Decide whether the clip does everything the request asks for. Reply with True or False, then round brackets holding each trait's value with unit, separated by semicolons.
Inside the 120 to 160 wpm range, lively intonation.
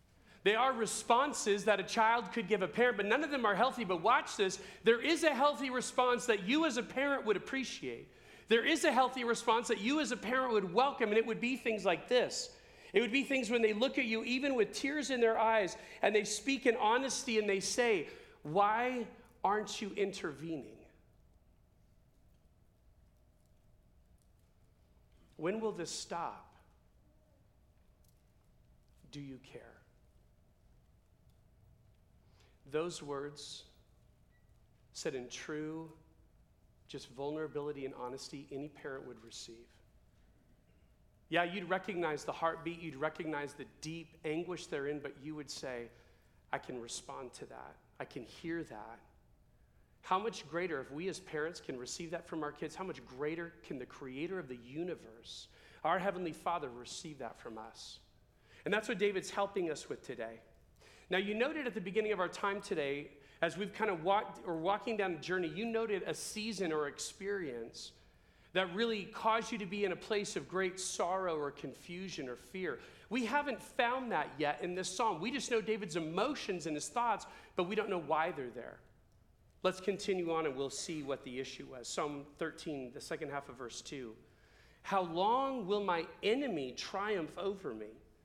False (170 wpm; 7.4 semitones)